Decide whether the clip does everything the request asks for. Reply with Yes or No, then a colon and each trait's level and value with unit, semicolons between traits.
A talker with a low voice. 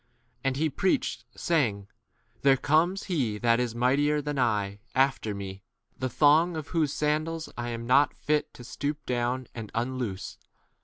Yes: low, 130 Hz